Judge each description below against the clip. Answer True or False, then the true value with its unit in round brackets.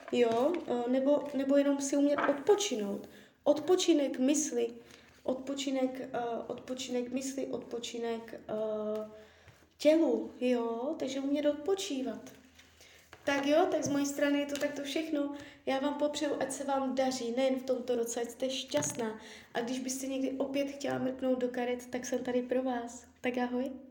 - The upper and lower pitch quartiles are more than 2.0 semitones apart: True (2.6 semitones)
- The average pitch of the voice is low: False (265 Hz)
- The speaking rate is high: False (145 wpm)